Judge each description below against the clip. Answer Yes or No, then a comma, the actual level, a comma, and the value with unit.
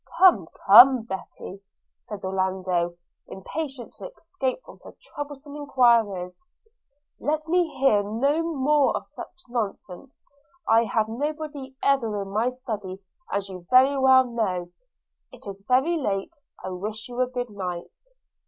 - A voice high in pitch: Yes, high, 240 Hz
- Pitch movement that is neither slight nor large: No, wide, 6.0 semitones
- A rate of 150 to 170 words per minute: No, average, 140 wpm